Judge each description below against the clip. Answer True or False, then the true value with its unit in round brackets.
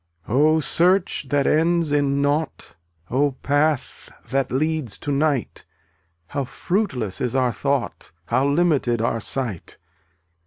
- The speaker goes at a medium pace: False (125 wpm)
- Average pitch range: True (3.3 semitones)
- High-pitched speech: False (140 Hz)